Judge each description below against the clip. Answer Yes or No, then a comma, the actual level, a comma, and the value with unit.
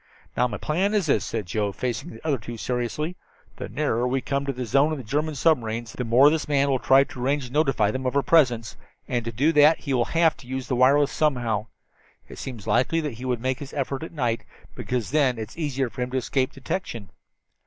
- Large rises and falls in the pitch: No, average, 3.6 semitones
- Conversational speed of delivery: No, fast, 240 wpm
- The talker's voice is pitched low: Yes, low, 130 Hz